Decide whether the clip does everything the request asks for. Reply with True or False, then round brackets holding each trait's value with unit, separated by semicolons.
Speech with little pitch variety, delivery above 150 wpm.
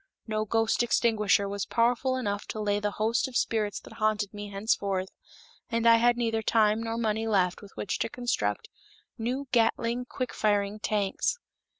True (2.2 semitones; 170 wpm)